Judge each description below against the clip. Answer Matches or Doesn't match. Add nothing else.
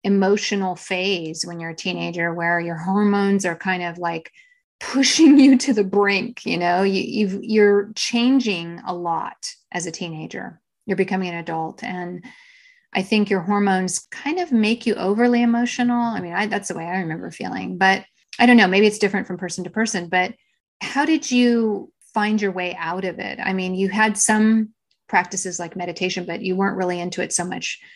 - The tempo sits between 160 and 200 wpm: Matches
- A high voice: Matches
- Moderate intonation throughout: Matches